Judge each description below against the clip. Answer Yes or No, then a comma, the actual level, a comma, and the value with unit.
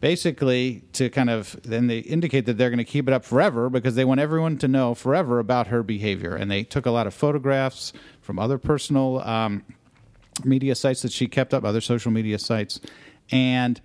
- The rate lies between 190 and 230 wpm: Yes, fast, 205 wpm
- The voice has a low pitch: Yes, low, 125 Hz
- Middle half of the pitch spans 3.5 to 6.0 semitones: No, average, 2.8 semitones